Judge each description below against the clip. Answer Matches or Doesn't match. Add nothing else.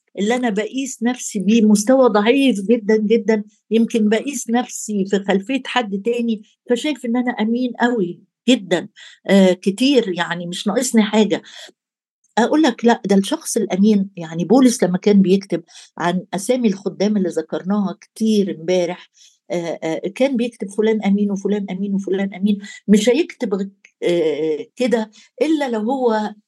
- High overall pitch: Matches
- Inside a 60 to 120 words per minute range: Doesn't match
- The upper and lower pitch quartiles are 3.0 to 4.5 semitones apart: Matches